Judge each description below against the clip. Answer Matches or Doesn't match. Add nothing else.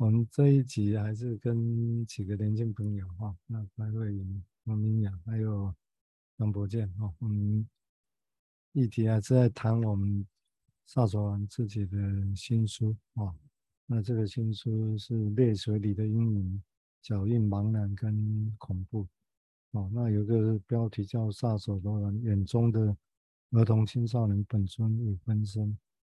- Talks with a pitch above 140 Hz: Doesn't match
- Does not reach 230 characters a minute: Matches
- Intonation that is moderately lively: Doesn't match